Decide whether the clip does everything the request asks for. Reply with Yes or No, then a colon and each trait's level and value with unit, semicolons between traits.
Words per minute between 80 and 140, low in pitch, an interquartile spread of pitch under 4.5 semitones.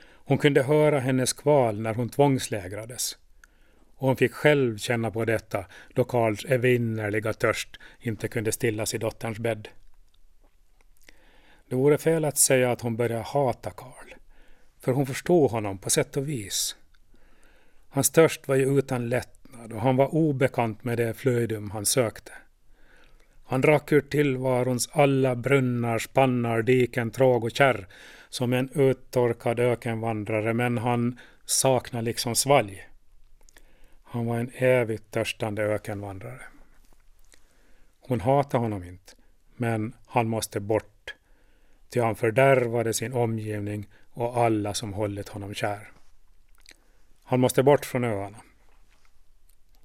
Yes: average, 130 wpm; low, 120 Hz; average, 3.1 semitones